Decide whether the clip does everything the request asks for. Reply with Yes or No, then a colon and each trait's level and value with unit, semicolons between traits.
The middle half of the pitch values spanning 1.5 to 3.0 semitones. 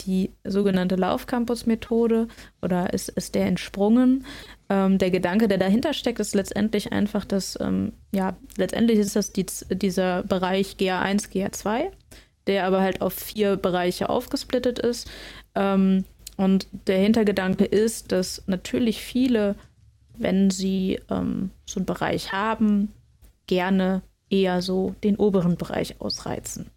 Yes: narrow, 2.6 semitones